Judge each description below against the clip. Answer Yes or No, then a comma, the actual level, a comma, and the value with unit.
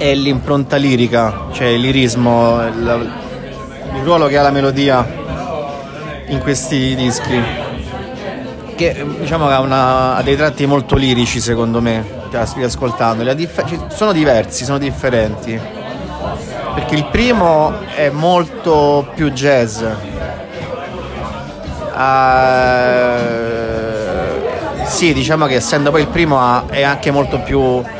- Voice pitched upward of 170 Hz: No, low, 130 Hz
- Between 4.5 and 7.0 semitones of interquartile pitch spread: No, average, 3.3 semitones